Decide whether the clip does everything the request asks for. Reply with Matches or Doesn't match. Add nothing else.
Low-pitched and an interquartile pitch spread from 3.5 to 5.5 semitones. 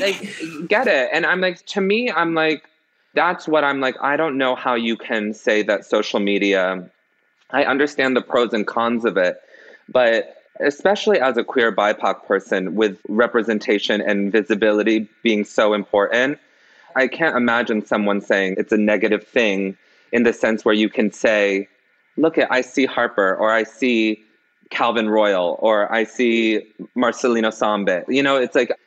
Matches